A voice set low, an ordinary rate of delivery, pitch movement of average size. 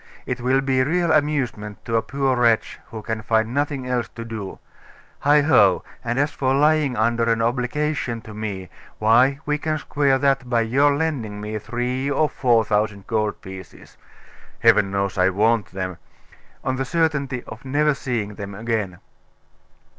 Yes: low, 120 Hz; average, 160 wpm; average, 4.4 semitones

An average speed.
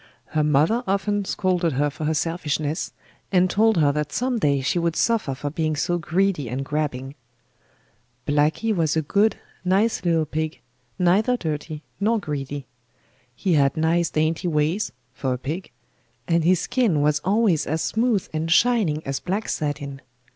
Yes: average, 160 wpm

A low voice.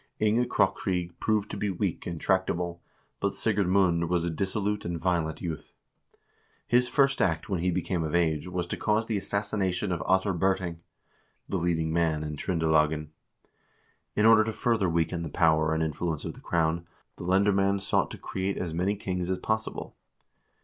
Yes: very low, 90 Hz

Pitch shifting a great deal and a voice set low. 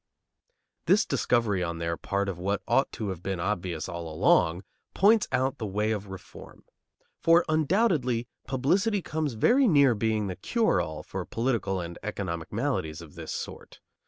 Yes: wide, 7.7 semitones; low, 105 Hz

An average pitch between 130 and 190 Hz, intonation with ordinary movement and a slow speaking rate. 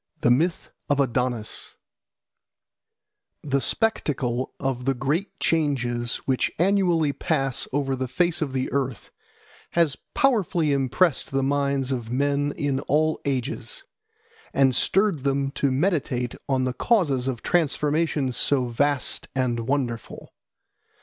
Yes: medium, 140 Hz; average, 3.0 semitones; slow, 125 wpm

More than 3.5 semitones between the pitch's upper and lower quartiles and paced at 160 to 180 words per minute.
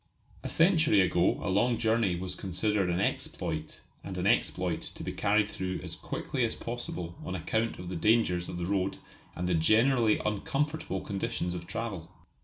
Yes: average, 4.3 semitones; average, 175 wpm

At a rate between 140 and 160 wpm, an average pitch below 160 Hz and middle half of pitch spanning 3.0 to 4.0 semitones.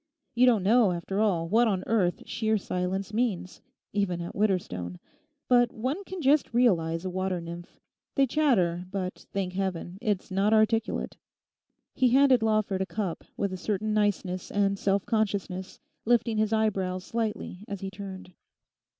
No: average, 150 wpm; high, 200 Hz; average, 3.3 semitones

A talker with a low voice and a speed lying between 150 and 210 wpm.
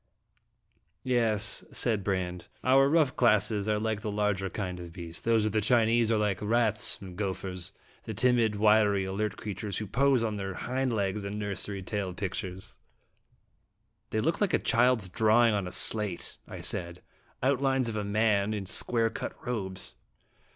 Yes: low, 105 Hz; average, 170 wpm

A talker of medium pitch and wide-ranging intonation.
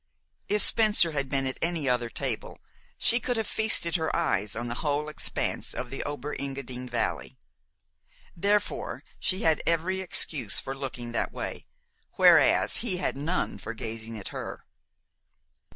Yes: medium, 145 Hz; wide, 6.3 semitones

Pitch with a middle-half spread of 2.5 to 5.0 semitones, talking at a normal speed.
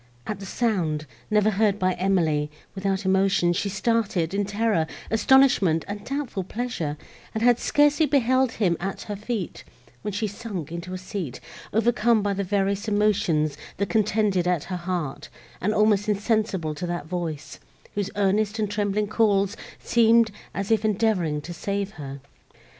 Yes: average, 3.3 semitones; average, 155 wpm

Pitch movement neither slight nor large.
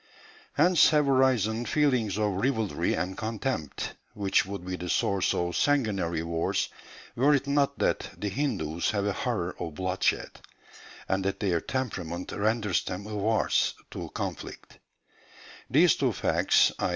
No: wide, 6.0 semitones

